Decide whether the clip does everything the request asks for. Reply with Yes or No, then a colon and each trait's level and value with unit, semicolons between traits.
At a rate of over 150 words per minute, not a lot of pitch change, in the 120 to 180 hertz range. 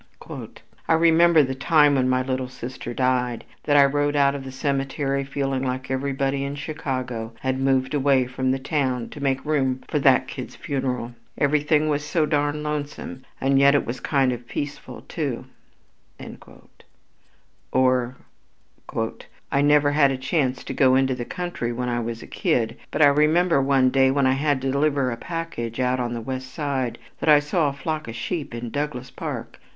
Yes: average, 185 wpm; narrow, 2.2 semitones; low, 135 Hz